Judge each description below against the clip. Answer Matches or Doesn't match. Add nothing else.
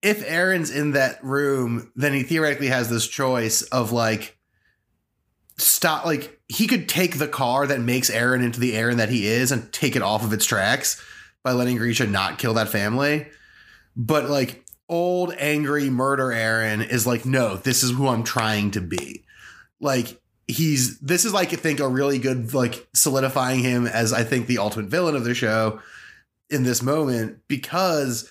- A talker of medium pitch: Doesn't match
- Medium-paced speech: Matches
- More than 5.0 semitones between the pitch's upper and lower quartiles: Doesn't match